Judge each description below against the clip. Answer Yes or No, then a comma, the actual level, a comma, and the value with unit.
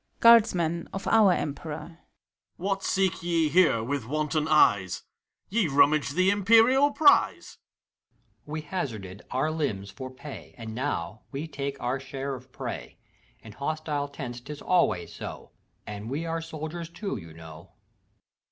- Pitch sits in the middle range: Yes, medium, 150 Hz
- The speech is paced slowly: No, average, 145 wpm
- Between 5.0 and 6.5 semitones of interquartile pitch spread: Yes, wide, 5.4 semitones